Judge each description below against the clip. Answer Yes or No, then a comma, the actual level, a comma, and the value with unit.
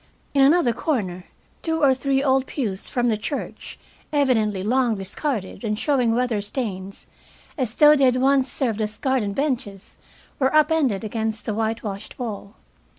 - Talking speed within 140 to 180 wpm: Yes, average, 155 wpm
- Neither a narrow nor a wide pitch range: Yes, average, 4.4 semitones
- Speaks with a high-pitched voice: Yes, high, 245 Hz